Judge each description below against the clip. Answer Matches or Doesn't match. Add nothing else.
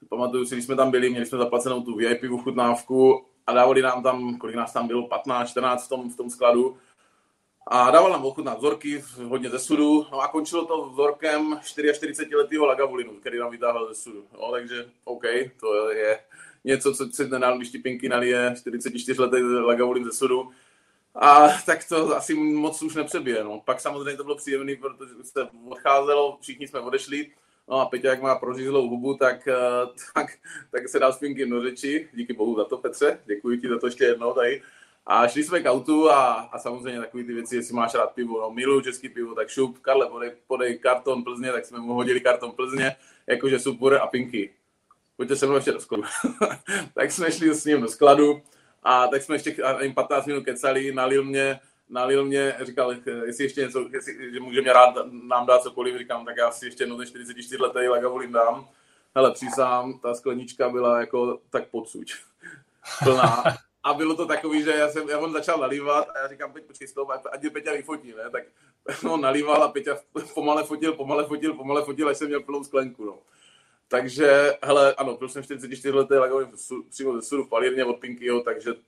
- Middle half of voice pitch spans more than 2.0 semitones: Matches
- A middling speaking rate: Doesn't match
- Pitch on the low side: Matches